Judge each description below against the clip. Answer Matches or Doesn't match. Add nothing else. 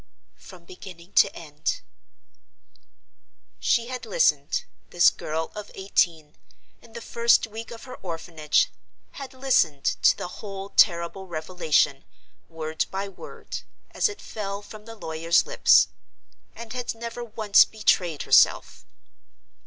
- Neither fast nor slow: Doesn't match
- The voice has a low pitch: Doesn't match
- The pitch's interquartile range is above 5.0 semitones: Matches